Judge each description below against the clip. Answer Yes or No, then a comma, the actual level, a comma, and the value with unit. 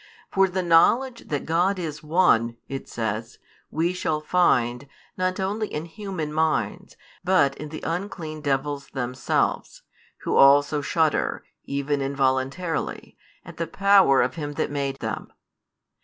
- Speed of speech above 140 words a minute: No, slow, 135 wpm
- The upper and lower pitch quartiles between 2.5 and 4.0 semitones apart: No, average, 4.8 semitones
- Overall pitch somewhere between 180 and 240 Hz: No, medium, 155 Hz